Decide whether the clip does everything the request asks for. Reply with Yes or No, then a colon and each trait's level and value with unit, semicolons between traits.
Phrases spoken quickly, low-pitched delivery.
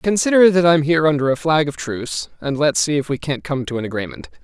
No: fast, 255 wpm; medium, 145 Hz